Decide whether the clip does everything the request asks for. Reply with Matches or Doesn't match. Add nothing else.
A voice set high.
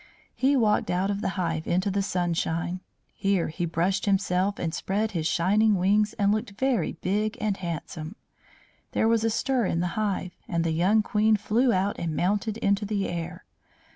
Matches